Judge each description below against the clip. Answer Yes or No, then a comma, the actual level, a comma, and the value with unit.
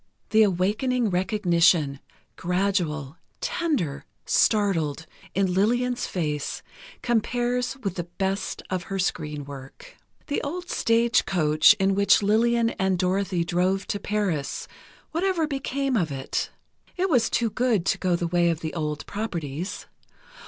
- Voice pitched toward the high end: Yes, high, 195 Hz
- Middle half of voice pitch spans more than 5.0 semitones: Yes, wide, 5.4 semitones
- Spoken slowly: Yes, slow, 130 wpm